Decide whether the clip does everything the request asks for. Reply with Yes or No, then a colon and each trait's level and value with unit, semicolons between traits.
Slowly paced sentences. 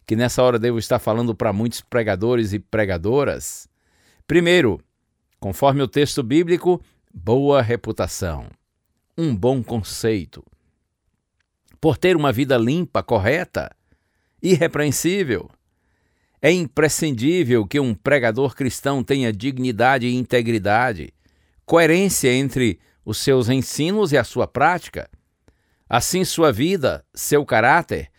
Yes: slow, 110 wpm